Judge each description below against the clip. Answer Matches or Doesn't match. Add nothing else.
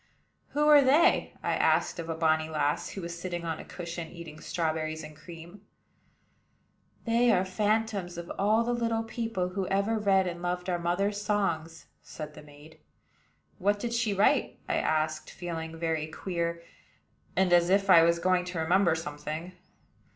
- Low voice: Doesn't match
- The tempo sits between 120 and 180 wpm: Matches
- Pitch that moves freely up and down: Doesn't match